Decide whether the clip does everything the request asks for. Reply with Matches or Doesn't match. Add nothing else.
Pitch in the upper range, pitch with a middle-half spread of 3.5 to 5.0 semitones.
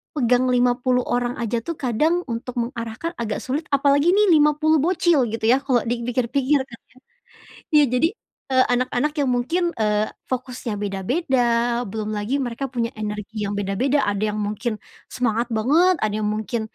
Matches